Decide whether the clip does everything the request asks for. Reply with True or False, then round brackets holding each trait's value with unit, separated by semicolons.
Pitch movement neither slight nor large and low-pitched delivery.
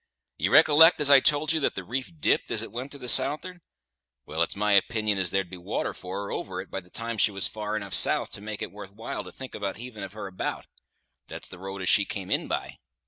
True (4.6 semitones; 105 Hz)